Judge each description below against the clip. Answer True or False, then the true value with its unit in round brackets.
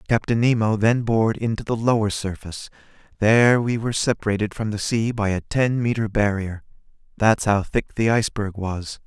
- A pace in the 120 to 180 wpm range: True (170 wpm)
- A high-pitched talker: False (110 Hz)